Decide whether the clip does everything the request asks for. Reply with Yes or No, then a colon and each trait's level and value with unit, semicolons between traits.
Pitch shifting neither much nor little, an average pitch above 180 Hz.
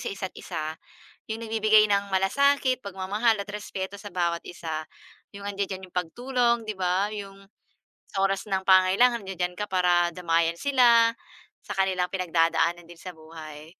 Yes: average, 3.1 semitones; high, 190 Hz